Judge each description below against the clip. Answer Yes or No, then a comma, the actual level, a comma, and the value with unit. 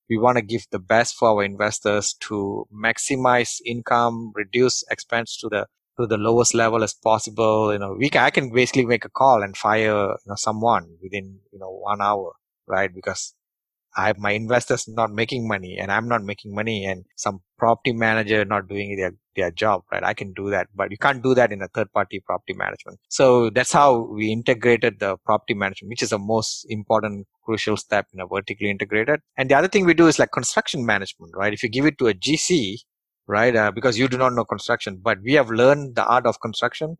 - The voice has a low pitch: Yes, low, 110 Hz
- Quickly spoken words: Yes, fast, 215 wpm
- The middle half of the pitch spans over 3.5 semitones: No, average, 3.1 semitones